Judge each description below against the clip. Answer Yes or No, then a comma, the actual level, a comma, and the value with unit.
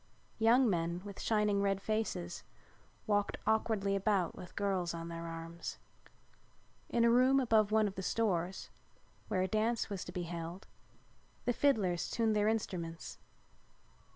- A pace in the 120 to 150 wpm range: Yes, average, 145 wpm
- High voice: Yes, high, 200 Hz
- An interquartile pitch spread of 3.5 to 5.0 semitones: Yes, average, 4.0 semitones